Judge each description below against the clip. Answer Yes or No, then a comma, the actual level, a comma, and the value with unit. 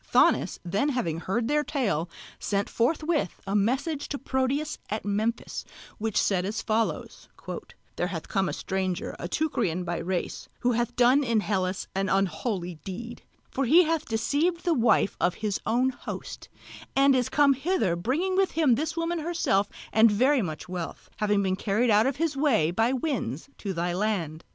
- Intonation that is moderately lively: No, wide, 6.6 semitones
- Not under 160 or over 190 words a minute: Yes, average, 175 wpm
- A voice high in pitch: Yes, high, 225 Hz